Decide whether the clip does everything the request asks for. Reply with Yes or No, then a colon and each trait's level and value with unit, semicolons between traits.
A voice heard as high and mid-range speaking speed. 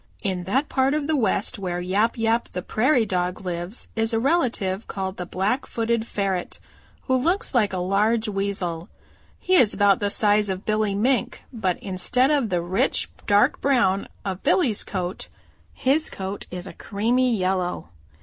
Yes: high, 205 Hz; average, 165 wpm